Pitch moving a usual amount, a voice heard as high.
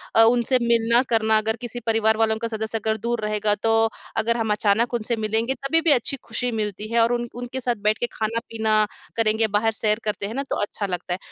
No: narrow, 1.6 semitones; high, 225 Hz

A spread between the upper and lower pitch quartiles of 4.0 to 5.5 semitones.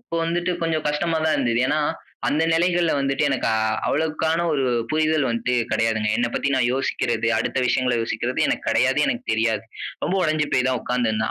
Yes: average, 4.6 semitones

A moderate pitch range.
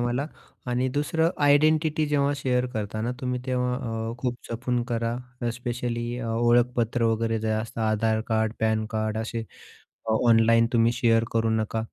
No: narrow, 1.9 semitones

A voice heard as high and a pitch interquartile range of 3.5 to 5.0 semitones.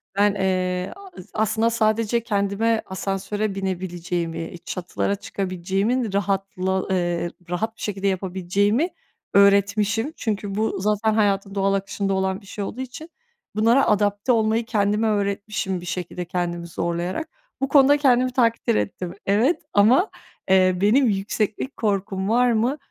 No: high, 200 Hz; average, 2.8 semitones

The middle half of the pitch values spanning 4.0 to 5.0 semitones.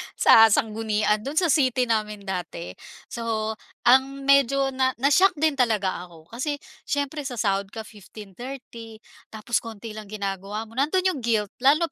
Yes: average, 4.4 semitones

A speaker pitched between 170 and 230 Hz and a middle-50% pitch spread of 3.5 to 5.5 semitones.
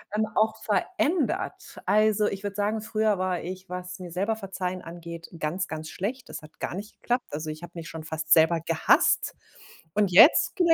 Yes: medium, 185 Hz; average, 4.2 semitones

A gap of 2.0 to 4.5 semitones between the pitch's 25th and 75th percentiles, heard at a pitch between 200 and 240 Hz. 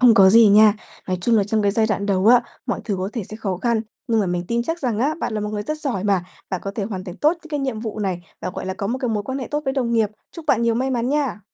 Yes: average, 3.8 semitones; high, 220 Hz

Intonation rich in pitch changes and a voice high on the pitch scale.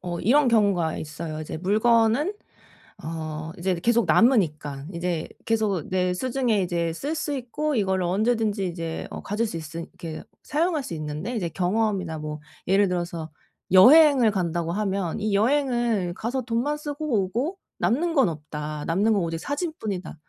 Yes: wide, 6.1 semitones; high, 195 Hz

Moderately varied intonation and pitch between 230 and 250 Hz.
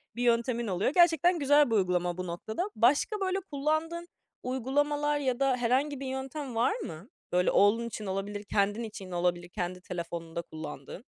No: wide, 7.9 semitones; high, 235 Hz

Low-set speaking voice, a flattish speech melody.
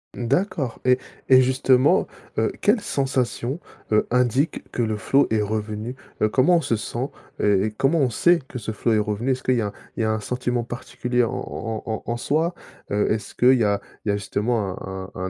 No: low, 120 Hz; average, 3.4 semitones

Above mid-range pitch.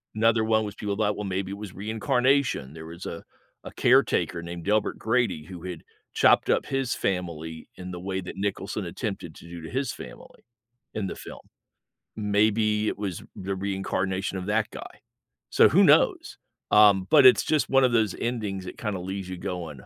No: low, 100 Hz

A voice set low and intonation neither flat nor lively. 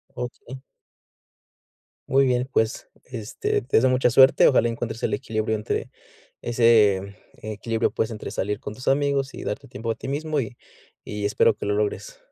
Yes: low, 115 Hz; average, 3.5 semitones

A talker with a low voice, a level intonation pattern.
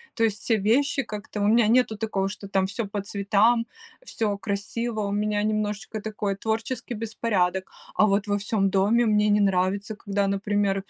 No: high, 210 Hz; narrow, 1.8 semitones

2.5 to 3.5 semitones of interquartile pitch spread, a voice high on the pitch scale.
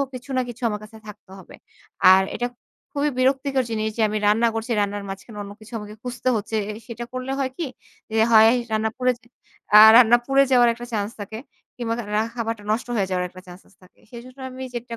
Yes: average, 3.2 semitones; high, 225 Hz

